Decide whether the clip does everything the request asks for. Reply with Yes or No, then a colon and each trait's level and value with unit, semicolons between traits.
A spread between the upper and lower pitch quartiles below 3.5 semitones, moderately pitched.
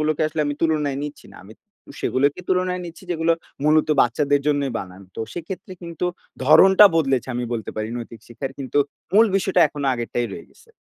No: average, 4.6 semitones; medium, 150 Hz